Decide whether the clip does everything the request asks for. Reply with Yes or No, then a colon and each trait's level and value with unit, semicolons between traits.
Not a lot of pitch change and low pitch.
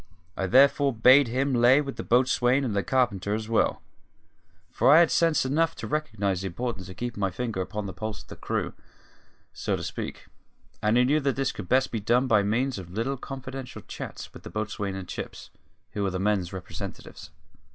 No: average, 4.8 semitones; low, 120 Hz